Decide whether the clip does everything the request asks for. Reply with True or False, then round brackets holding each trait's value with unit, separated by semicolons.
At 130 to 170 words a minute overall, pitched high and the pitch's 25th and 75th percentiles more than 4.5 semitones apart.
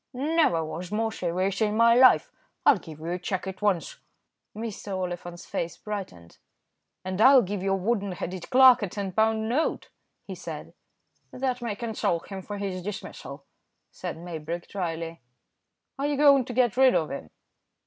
True (165 wpm; 200 Hz; 4.9 semitones)